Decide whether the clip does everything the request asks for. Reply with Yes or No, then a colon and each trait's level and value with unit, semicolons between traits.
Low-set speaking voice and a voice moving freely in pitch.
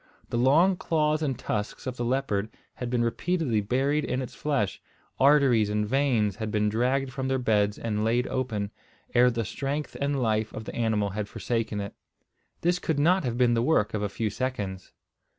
No: low, 120 Hz; average, 4.3 semitones